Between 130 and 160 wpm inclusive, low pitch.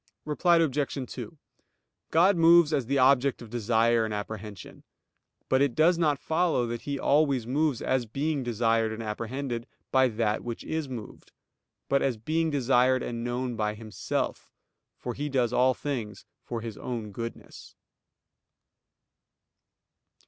Yes: average, 140 wpm; low, 125 Hz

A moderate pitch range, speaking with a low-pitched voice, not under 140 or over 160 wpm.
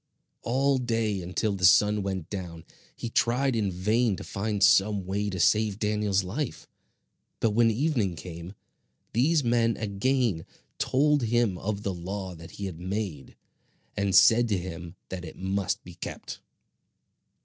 Yes: average, 3.9 semitones; low, 105 Hz; average, 150 wpm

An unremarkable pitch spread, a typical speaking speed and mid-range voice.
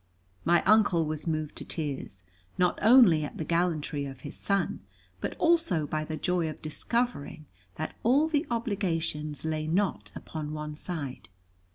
Yes: average, 4.7 semitones; average, 155 wpm; medium, 160 Hz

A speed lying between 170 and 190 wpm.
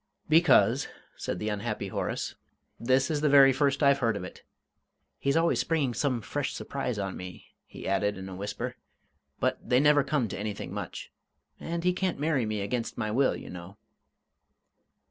Yes: average, 175 wpm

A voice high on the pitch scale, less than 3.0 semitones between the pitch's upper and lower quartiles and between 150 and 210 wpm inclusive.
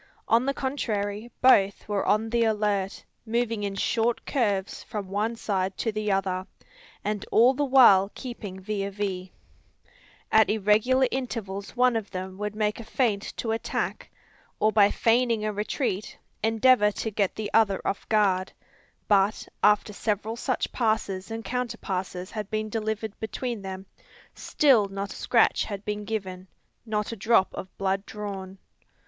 Yes: high, 210 Hz; narrow, 2.4 semitones; average, 155 wpm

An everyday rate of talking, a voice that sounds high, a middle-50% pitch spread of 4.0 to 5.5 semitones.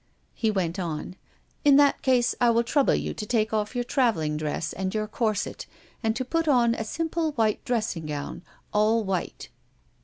Yes: average, 180 wpm; high, 220 Hz; average, 4.5 semitones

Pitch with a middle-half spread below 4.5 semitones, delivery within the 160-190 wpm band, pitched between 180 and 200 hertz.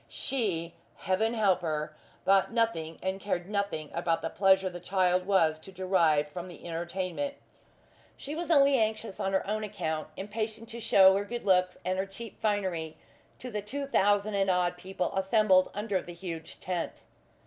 Yes: average, 3.3 semitones; average, 170 wpm; high, 190 Hz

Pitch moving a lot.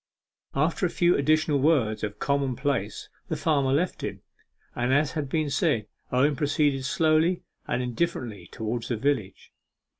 No: average, 4.1 semitones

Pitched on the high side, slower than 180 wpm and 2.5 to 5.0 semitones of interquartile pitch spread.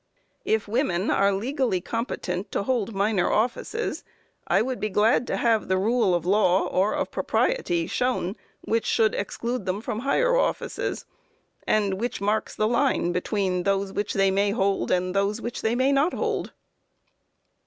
Yes: high, 210 Hz; average, 160 wpm; average, 3.7 semitones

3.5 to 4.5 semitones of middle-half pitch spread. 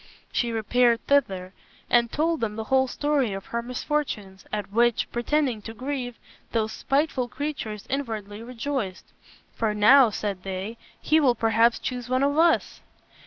Yes: average, 4.2 semitones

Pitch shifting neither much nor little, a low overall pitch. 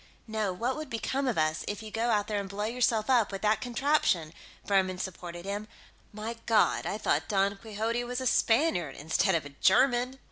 No: average, 3.7 semitones; high, 215 Hz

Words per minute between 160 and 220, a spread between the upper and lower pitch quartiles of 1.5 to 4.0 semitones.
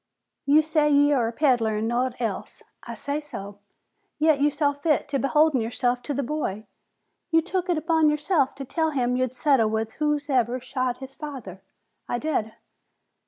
Yes: average, 175 wpm; average, 3.7 semitones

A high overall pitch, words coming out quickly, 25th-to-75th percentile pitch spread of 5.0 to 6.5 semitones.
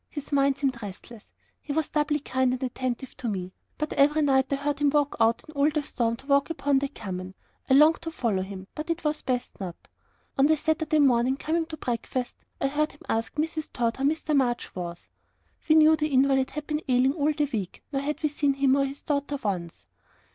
No: very high, 275 Hz; fast, 220 wpm; average, 3.7 semitones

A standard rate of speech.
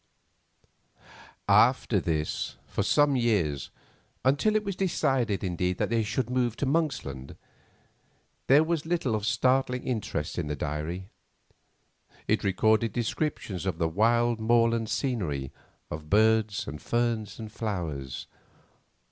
No: slow, 115 wpm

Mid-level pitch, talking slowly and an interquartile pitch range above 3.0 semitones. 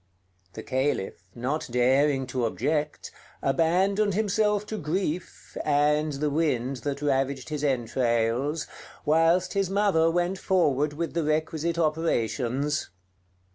Yes: medium, 150 Hz; slow, 115 wpm; average, 4.0 semitones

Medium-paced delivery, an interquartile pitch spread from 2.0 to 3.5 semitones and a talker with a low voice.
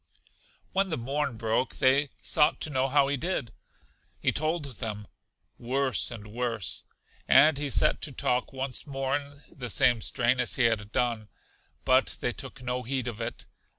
Yes: average, 170 wpm; average, 3.1 semitones; low, 130 Hz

